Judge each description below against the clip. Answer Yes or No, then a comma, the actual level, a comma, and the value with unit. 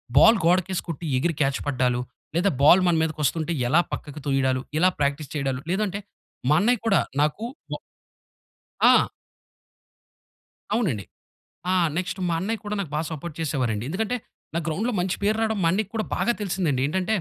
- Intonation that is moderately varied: No, wide, 5.8 semitones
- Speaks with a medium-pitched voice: Yes, medium, 170 Hz